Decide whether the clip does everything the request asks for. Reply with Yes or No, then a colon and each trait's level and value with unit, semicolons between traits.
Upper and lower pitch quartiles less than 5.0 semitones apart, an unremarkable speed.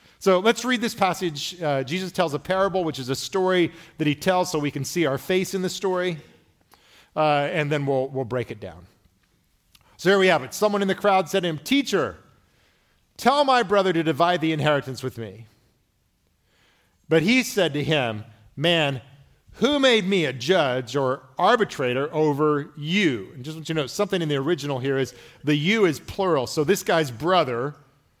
No: wide, 5.6 semitones; average, 195 wpm